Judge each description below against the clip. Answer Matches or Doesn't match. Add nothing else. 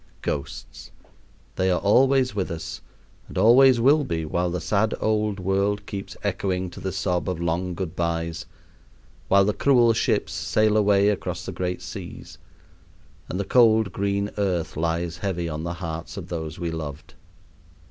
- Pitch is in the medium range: Doesn't match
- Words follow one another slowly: Doesn't match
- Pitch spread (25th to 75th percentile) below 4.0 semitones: Matches